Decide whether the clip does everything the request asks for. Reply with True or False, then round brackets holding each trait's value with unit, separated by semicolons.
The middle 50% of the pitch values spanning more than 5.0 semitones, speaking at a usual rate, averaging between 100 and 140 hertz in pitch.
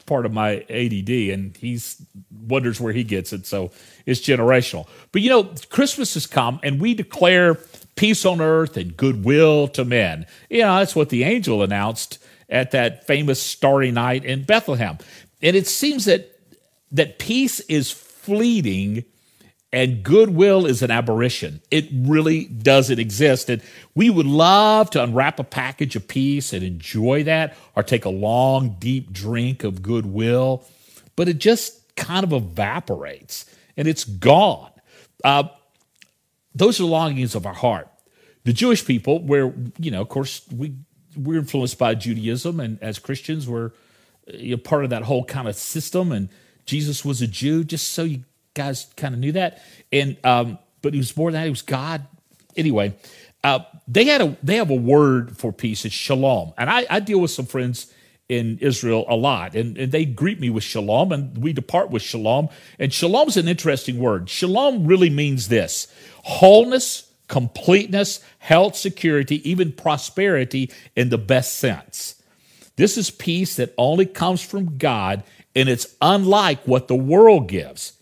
True (5.4 semitones; 170 wpm; 135 Hz)